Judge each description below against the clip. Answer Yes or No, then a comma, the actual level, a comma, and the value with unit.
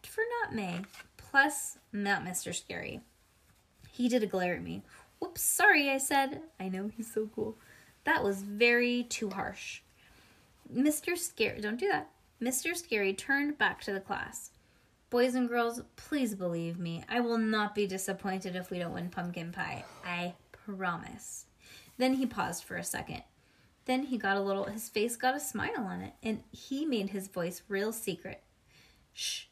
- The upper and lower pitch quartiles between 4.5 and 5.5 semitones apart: Yes, average, 5.0 semitones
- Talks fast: No, average, 170 wpm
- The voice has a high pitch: Yes, high, 215 Hz